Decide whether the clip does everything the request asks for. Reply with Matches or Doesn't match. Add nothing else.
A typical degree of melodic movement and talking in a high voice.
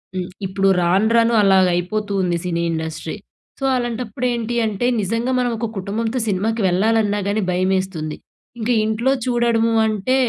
Matches